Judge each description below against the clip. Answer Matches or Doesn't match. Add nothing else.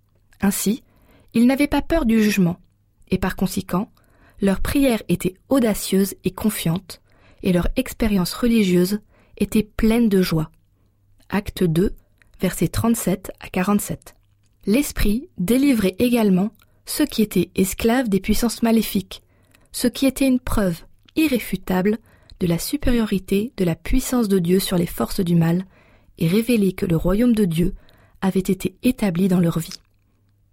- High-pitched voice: Matches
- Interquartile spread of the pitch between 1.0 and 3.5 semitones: Doesn't match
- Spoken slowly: Matches